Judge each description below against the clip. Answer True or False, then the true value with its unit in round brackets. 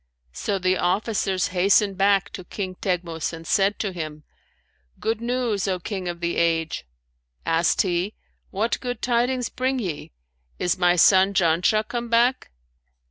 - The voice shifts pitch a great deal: False (3.9 semitones)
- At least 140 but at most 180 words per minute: True (145 wpm)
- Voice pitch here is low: False (190 Hz)